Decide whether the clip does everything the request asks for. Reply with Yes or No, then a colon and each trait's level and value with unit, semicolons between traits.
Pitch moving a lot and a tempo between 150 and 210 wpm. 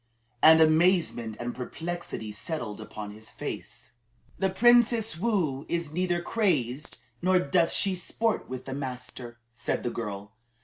No: wide, 7.2 semitones; slow, 135 wpm